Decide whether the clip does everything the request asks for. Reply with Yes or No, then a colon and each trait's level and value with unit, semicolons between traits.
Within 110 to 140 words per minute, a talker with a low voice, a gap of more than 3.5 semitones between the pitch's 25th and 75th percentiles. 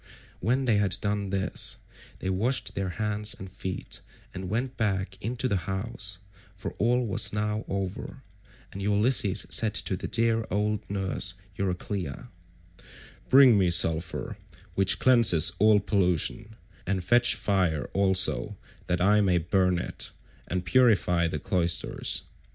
No: slow, 135 wpm; low, 100 Hz; average, 2.8 semitones